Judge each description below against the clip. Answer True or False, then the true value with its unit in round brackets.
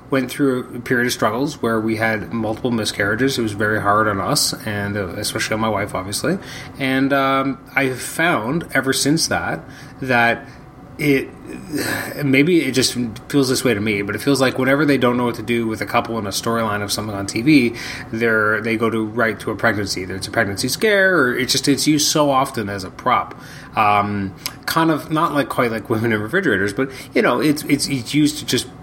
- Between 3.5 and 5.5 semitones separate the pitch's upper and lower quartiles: True (3.9 semitones)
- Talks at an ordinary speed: False (220 wpm)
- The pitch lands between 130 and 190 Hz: False (120 Hz)